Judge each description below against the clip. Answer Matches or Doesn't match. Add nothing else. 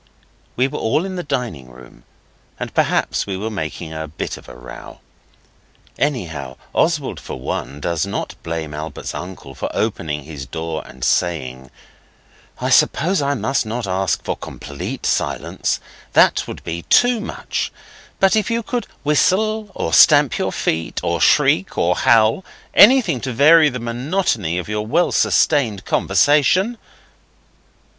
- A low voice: Matches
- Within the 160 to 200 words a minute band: Doesn't match